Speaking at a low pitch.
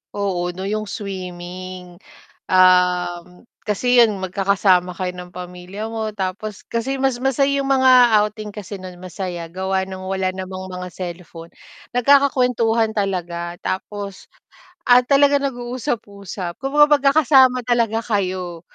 No: high, 200 Hz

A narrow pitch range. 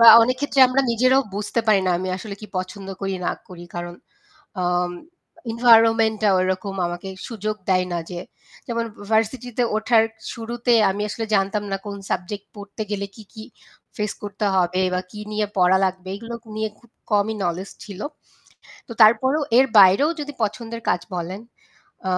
No: average, 3.3 semitones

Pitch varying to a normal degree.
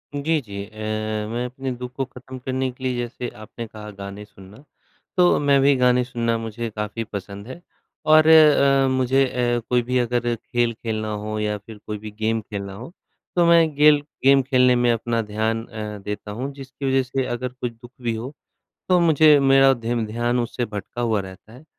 Yes: average, 3.3 semitones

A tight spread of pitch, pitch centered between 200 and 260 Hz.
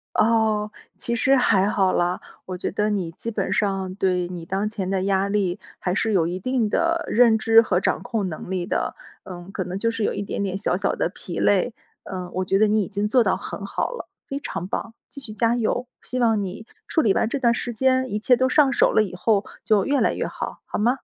No: average, 3.7 semitones; high, 210 Hz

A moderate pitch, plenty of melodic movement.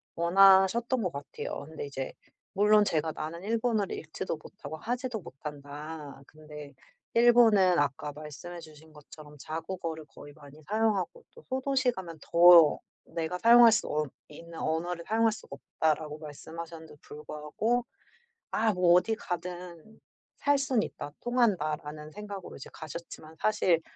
Yes: medium, 170 Hz; wide, 5.7 semitones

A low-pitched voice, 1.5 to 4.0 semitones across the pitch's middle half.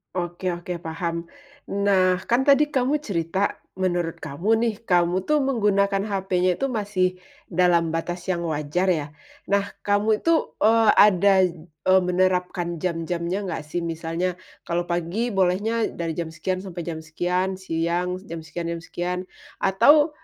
No: medium, 180 Hz; average, 2.9 semitones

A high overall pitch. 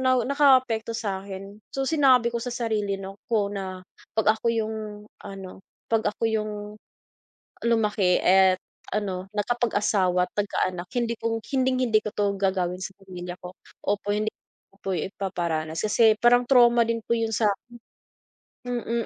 Yes: high, 215 Hz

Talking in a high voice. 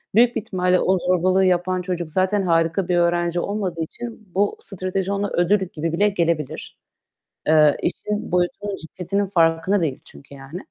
No: medium, 180 Hz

